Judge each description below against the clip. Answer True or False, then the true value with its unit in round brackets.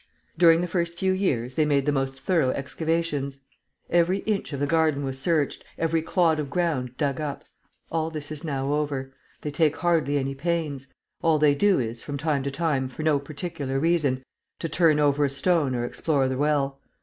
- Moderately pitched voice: True (150 Hz)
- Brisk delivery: False (195 wpm)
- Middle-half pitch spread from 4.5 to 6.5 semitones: False (3.2 semitones)